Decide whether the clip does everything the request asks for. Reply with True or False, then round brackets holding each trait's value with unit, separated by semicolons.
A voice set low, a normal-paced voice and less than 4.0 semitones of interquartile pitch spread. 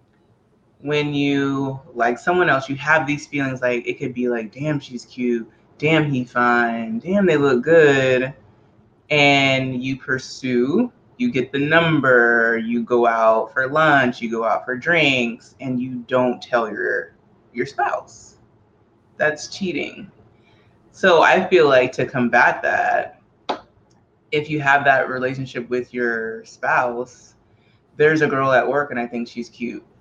True (125 Hz; 150 wpm; 3.1 semitones)